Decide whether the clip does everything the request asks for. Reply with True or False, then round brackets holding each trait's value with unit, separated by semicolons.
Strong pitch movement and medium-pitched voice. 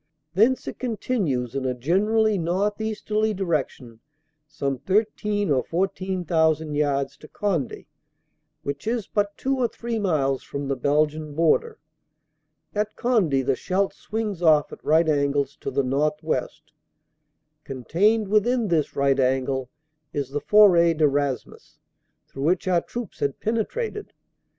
True (7.0 semitones; 165 Hz)